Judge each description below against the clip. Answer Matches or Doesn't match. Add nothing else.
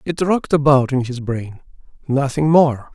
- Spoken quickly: Doesn't match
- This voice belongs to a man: Matches